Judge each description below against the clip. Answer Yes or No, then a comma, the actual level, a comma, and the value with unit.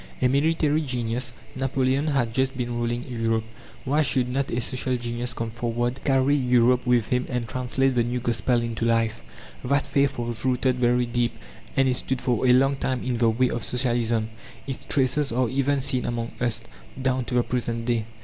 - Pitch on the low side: Yes, low, 125 Hz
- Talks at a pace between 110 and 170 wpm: No, average, 190 wpm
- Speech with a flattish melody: Yes, narrow, 1.9 semitones